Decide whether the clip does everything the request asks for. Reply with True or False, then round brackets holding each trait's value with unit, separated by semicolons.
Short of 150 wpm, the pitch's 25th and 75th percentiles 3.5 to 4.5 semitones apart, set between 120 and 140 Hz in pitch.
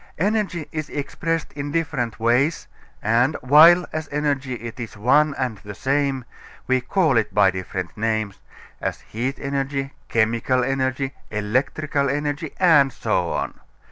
True (140 wpm; 4.1 semitones; 135 Hz)